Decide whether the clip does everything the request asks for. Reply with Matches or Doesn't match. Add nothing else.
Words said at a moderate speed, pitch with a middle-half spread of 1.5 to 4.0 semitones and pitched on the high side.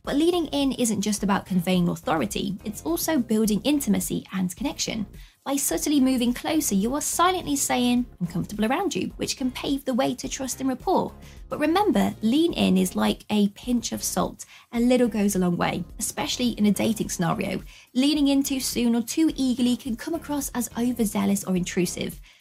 Doesn't match